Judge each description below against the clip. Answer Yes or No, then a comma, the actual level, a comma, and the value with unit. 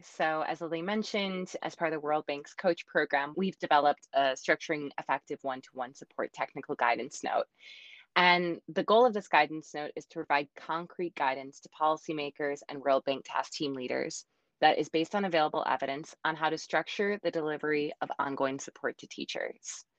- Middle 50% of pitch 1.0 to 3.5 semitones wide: Yes, average, 3.1 semitones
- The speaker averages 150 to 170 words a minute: No, average, 185 wpm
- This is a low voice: No, medium, 155 Hz